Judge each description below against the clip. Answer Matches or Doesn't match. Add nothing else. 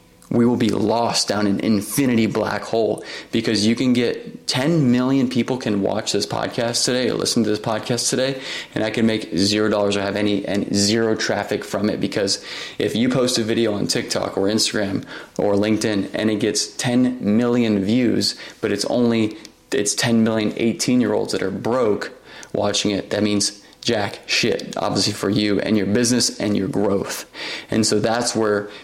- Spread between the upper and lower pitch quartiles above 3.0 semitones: Doesn't match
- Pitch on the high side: Doesn't match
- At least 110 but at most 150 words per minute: Doesn't match